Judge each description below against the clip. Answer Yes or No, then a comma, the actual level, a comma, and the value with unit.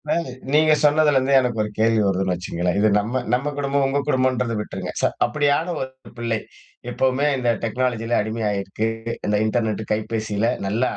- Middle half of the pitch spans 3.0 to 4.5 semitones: Yes, average, 3.8 semitones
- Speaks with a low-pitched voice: Yes, low, 120 Hz